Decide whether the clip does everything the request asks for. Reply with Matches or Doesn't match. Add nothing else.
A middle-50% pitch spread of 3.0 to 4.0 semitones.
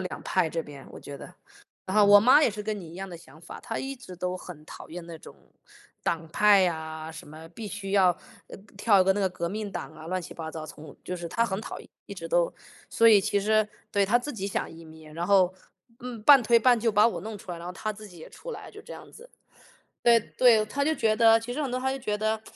Doesn't match